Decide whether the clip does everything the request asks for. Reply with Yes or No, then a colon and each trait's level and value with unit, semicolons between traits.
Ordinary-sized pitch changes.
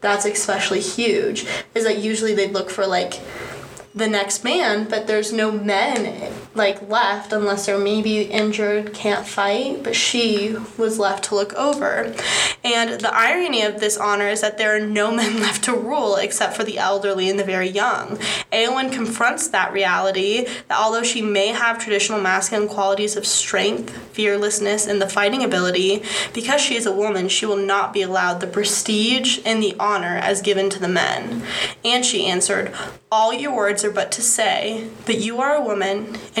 No: narrow, 1.8 semitones